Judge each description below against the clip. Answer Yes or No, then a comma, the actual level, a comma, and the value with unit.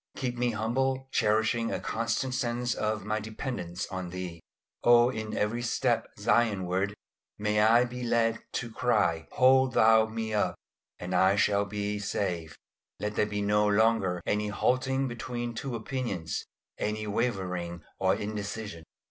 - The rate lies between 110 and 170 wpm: Yes, average, 145 wpm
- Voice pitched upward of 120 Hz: No, low, 110 Hz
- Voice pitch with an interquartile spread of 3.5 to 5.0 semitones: No, average, 2.8 semitones